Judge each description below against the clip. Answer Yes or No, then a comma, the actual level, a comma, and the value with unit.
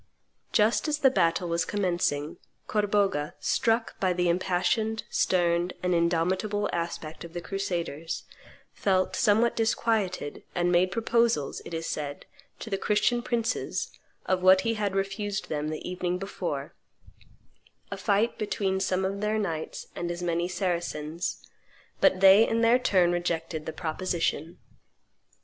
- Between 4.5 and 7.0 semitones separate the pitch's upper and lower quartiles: No, average, 3.4 semitones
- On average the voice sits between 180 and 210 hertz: Yes, medium, 185 Hz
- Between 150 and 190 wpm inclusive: No, average, 140 wpm